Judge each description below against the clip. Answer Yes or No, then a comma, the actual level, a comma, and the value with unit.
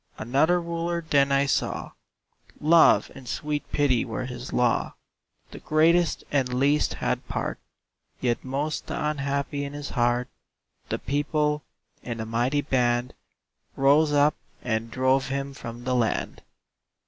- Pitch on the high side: No, medium, 140 Hz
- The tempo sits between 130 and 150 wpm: Yes, average, 140 wpm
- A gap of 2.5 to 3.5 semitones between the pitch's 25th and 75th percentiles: Yes, average, 3.1 semitones